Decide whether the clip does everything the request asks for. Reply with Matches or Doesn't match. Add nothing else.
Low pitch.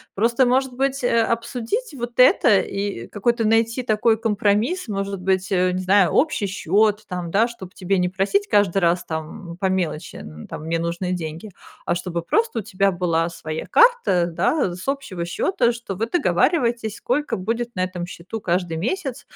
Doesn't match